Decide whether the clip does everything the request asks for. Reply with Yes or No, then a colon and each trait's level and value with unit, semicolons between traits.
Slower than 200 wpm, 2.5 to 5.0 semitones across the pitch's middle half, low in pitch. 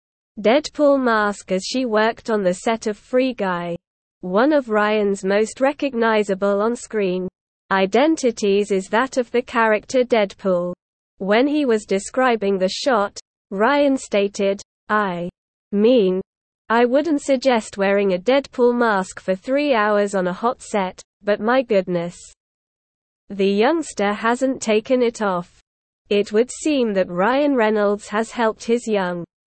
No: average, 140 wpm; average, 3.8 semitones; high, 215 Hz